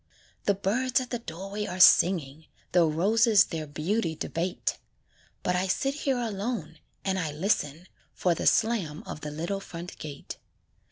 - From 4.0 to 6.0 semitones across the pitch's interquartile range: Yes, average, 5.0 semitones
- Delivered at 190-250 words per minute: No, average, 155 wpm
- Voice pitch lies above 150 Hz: Yes, medium, 185 Hz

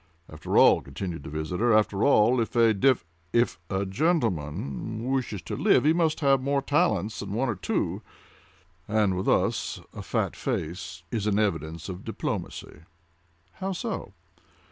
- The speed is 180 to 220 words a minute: No, average, 150 wpm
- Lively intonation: Yes, wide, 6.7 semitones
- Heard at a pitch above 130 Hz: No, low, 105 Hz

